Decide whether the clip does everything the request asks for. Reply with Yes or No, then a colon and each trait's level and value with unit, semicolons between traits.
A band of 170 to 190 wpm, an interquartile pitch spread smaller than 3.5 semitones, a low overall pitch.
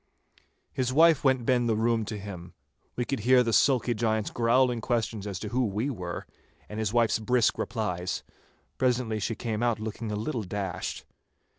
Yes: average, 175 wpm; average, 2.8 semitones; low, 115 Hz